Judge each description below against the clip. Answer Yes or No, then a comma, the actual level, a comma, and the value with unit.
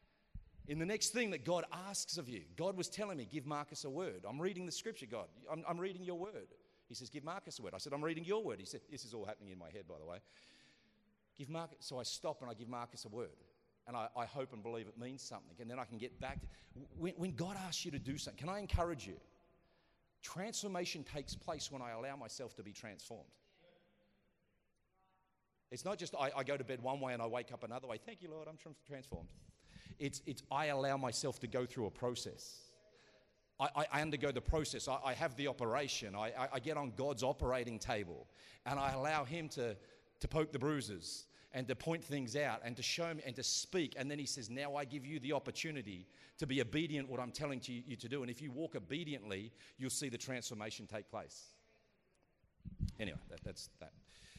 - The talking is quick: Yes, fast, 225 wpm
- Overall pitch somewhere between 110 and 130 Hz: No, medium, 140 Hz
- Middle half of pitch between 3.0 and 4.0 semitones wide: No, average, 4.4 semitones